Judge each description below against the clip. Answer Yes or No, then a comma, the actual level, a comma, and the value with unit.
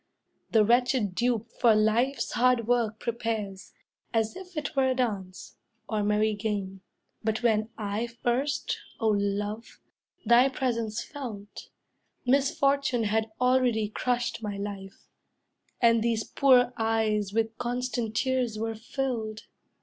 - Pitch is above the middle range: Yes, high, 225 Hz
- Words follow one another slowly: Yes, slow, 125 wpm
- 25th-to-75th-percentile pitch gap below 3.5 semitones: Yes, average, 2.7 semitones